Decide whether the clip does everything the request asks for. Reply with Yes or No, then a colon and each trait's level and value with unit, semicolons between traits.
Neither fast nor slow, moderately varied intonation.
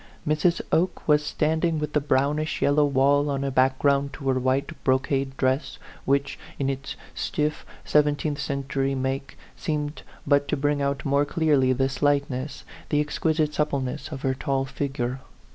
No: average, 160 wpm; narrow, 1.8 semitones